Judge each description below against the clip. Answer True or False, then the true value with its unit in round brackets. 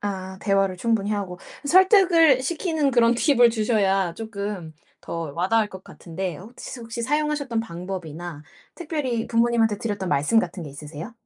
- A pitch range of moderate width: True (4.9 semitones)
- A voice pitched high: True (215 Hz)